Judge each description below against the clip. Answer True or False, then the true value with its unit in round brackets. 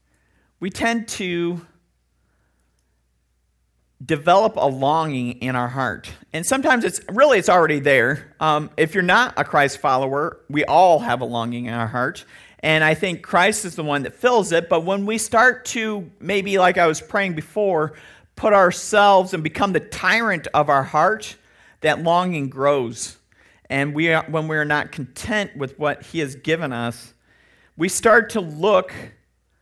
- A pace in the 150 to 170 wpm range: True (165 wpm)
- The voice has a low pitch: False (155 Hz)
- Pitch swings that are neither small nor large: False (6.1 semitones)